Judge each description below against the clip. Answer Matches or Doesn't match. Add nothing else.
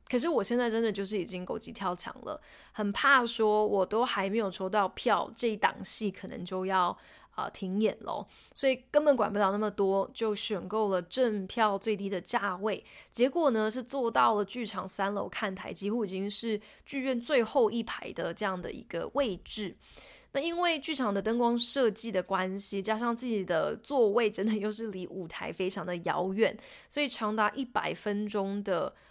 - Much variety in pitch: Doesn't match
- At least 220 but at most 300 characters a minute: Matches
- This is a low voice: Doesn't match